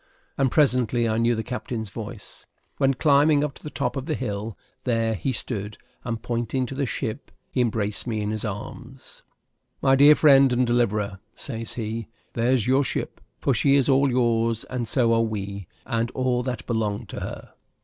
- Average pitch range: Yes, average, 3.1 semitones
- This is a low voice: Yes, low, 120 Hz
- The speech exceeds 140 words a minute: Yes, average, 185 wpm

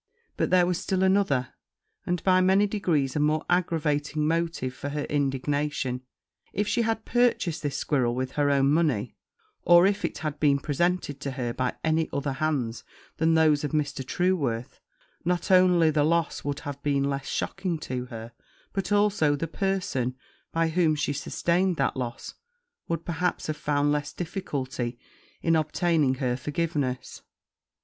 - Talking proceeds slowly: No, average, 160 wpm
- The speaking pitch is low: No, medium, 150 Hz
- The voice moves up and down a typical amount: Yes, average, 4.1 semitones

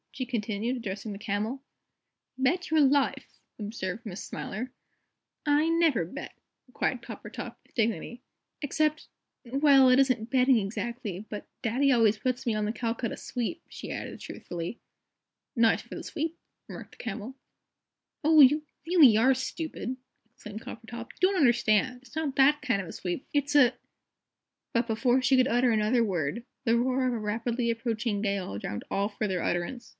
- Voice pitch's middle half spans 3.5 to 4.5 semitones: Yes, average, 3.8 semitones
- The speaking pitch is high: Yes, high, 240 Hz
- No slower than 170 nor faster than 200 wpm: No, average, 160 wpm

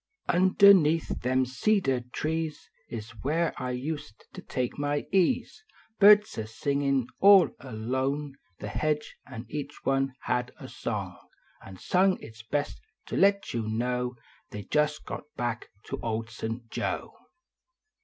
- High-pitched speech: No, medium, 140 Hz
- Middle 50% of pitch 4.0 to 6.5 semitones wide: Yes, average, 4.8 semitones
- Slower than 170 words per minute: Yes, slow, 135 wpm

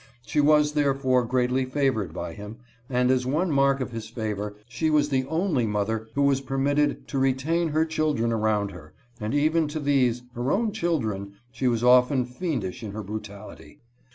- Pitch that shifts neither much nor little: Yes, average, 4.7 semitones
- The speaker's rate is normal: Yes, average, 180 wpm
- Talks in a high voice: No, low, 130 Hz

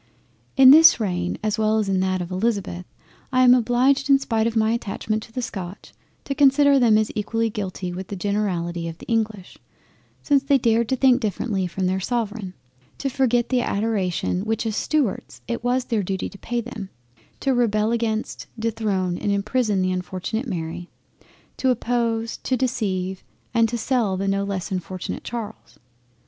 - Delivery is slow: No, average, 175 wpm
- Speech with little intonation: No, average, 4.2 semitones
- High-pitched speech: Yes, high, 220 Hz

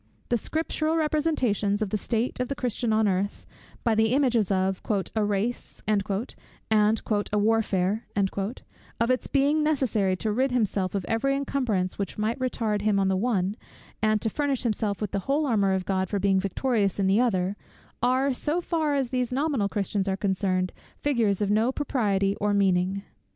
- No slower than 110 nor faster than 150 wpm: No, average, 175 wpm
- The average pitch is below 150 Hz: No, high, 215 Hz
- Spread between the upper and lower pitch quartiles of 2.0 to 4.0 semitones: No, average, 4.4 semitones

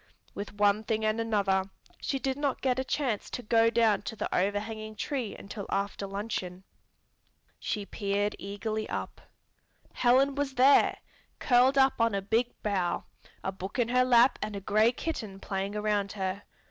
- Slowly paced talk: No, average, 165 wpm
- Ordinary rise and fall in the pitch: Yes, average, 3.5 semitones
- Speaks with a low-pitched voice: No, high, 215 Hz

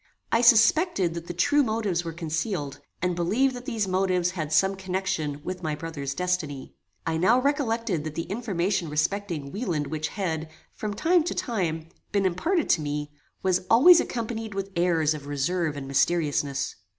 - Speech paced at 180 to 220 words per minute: No, average, 165 wpm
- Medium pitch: Yes, medium, 180 Hz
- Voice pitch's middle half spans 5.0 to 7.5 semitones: Yes, wide, 5.6 semitones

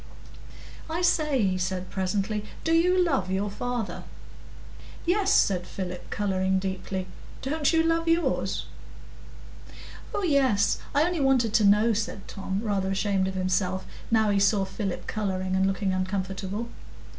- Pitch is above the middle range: Yes, high, 200 Hz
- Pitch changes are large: Yes, wide, 6.0 semitones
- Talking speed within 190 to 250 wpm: No, slow, 135 wpm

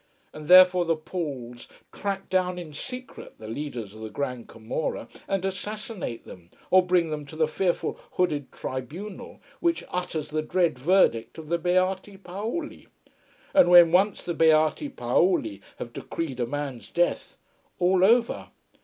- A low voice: No, medium, 170 Hz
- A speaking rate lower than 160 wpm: Yes, average, 150 wpm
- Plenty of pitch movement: No, average, 4.8 semitones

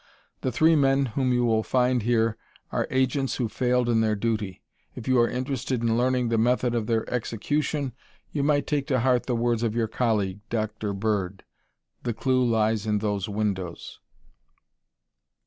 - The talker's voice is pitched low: Yes, low, 120 Hz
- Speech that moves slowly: No, average, 170 wpm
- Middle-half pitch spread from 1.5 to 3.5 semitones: Yes, average, 2.9 semitones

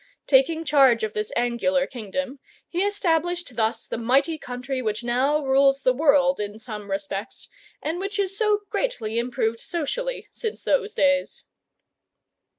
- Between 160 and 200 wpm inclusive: No, average, 145 wpm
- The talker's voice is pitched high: Yes, very high, 270 Hz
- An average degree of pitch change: No, wide, 5.7 semitones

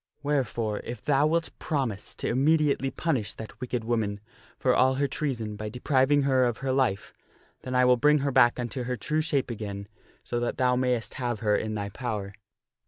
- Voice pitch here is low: Yes, low, 125 Hz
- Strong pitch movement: No, average, 3.6 semitones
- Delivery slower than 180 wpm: No, average, 190 wpm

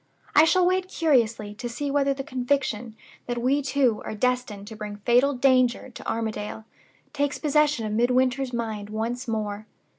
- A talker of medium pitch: No, high, 245 Hz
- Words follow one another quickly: No, average, 160 wpm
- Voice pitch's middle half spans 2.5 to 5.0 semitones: Yes, average, 4.1 semitones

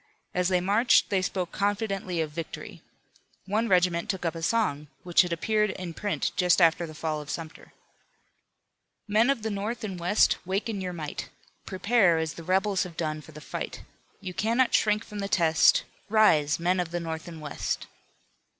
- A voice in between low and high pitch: Yes, medium, 180 Hz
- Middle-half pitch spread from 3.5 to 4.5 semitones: Yes, average, 3.8 semitones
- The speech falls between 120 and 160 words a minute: No, average, 185 wpm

